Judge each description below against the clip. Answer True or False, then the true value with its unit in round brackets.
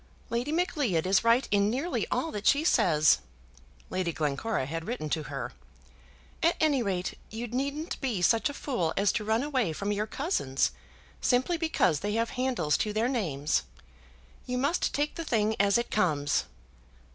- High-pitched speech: True (220 Hz)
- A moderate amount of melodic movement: False (6.9 semitones)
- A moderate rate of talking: True (170 wpm)